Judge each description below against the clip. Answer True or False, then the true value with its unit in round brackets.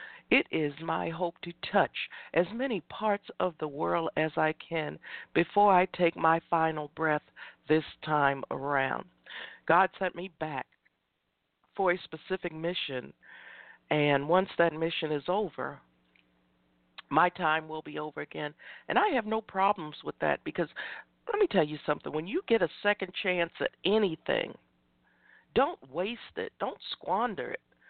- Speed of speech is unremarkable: True (155 wpm)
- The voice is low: False (160 Hz)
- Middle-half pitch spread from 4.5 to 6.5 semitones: False (3.8 semitones)